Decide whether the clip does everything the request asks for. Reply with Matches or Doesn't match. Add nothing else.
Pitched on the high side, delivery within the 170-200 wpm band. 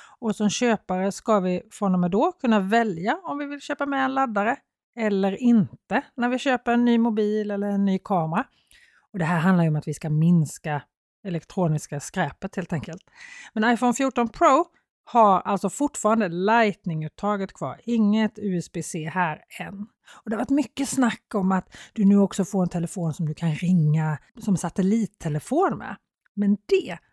Matches